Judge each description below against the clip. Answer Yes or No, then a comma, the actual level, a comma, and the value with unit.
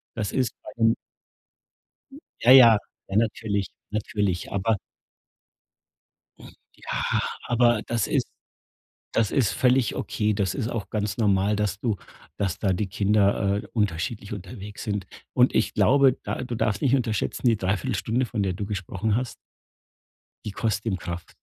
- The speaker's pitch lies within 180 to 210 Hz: No, low, 105 Hz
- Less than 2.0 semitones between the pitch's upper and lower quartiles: No, average, 2.7 semitones